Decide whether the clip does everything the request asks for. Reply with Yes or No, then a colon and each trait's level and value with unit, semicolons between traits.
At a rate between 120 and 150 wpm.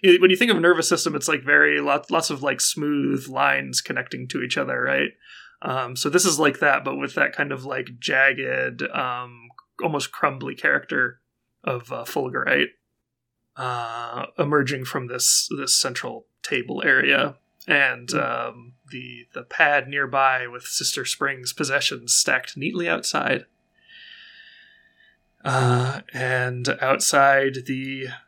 Yes: average, 140 wpm